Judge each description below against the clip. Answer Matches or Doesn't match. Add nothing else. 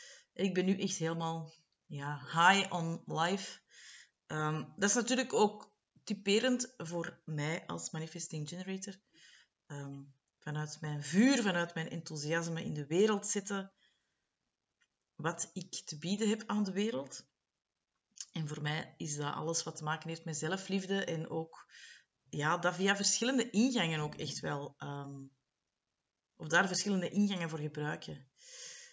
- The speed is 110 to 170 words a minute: Matches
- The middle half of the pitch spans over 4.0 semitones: Matches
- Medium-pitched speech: Matches